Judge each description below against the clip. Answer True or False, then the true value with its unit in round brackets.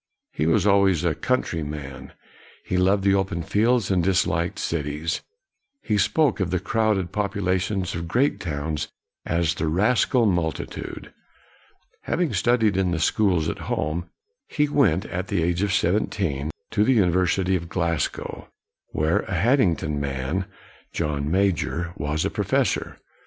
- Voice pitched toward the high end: False (90 Hz)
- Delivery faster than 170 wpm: False (150 wpm)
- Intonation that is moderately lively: True (3.9 semitones)